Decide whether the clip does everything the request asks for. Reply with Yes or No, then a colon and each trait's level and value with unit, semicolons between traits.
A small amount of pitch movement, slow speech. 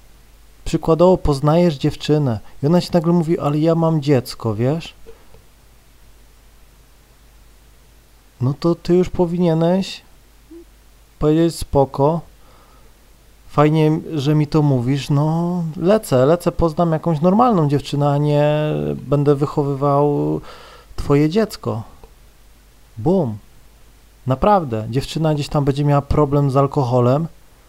No: average, 3.3 semitones; slow, 105 wpm